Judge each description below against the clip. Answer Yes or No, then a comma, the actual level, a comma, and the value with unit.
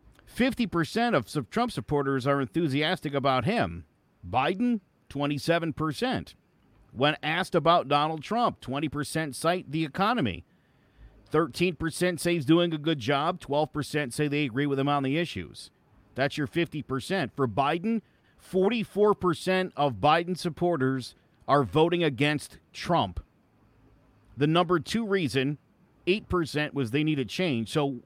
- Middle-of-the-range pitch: Yes, medium, 150 Hz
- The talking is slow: Yes, slow, 125 wpm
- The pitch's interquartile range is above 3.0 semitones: Yes, average, 4.2 semitones